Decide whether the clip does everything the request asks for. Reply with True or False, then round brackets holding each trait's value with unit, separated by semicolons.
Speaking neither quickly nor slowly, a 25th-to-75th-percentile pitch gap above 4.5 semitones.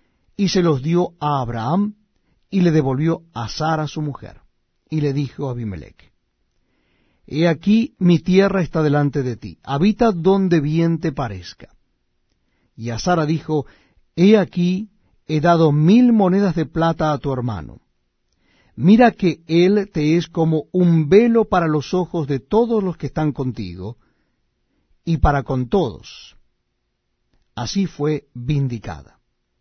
True (140 wpm; 5.1 semitones)